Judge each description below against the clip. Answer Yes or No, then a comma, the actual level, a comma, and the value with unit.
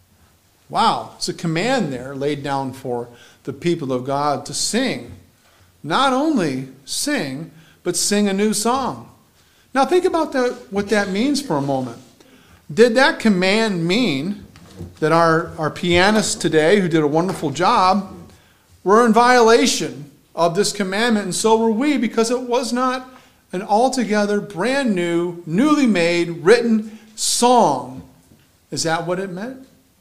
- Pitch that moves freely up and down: Yes, wide, 7.8 semitones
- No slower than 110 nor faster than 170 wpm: Yes, average, 145 wpm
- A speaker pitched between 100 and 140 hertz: No, high, 190 Hz